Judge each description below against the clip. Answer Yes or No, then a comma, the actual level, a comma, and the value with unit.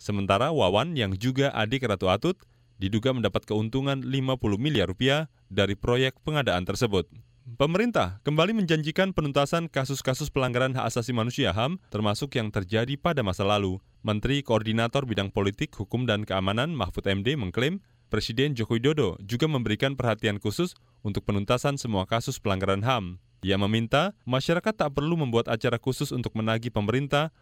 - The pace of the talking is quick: Yes, fast, 145 wpm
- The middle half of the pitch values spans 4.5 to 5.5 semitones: Yes, average, 4.8 semitones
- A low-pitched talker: Yes, low, 120 Hz